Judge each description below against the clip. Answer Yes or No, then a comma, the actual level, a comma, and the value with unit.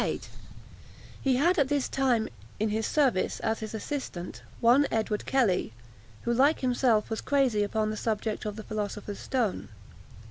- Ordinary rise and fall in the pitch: Yes, average, 3.8 semitones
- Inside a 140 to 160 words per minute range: Yes, average, 155 wpm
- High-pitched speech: Yes, high, 225 Hz